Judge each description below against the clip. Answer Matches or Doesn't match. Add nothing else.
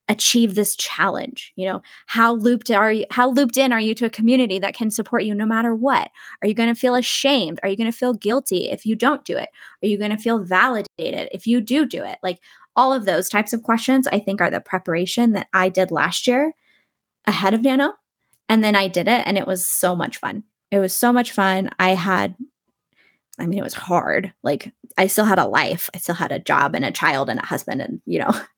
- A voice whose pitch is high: Matches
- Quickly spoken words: Matches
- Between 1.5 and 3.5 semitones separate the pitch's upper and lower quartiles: Doesn't match